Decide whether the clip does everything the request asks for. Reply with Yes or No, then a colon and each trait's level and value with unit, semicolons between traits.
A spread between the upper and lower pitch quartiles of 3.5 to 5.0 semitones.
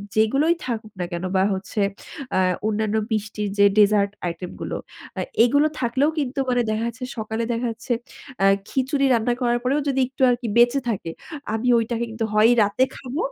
No: average, 3.0 semitones